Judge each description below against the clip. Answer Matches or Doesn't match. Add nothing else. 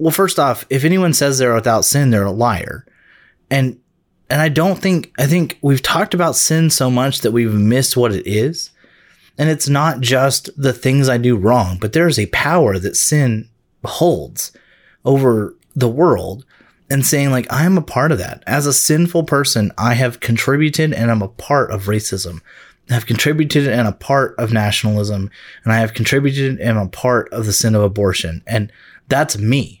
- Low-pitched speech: Matches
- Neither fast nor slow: Matches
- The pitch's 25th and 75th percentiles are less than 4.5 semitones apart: Doesn't match